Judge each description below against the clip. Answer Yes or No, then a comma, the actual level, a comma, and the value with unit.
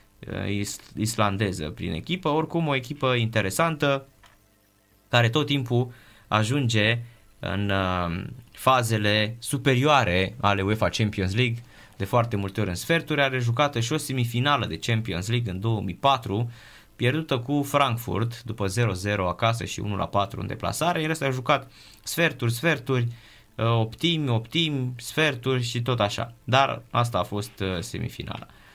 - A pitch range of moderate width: Yes, average, 4.6 semitones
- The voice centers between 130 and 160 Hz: No, low, 115 Hz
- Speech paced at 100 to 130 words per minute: Yes, average, 125 wpm